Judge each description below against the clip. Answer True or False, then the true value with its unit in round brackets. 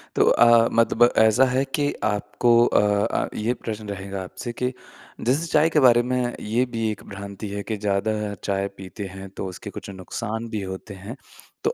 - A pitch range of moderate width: True (3.4 semitones)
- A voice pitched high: False (110 Hz)